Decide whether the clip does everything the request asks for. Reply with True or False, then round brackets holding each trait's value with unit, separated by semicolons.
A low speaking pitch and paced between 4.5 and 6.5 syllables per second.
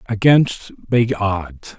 False (105 Hz; 2.5 syllables/s)